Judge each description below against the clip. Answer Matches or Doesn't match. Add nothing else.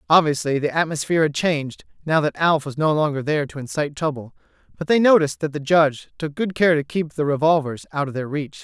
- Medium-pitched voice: Matches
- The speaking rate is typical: Doesn't match